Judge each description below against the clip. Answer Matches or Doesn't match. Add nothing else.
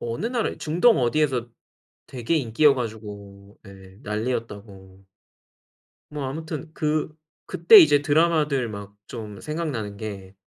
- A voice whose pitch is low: Matches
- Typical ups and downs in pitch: Doesn't match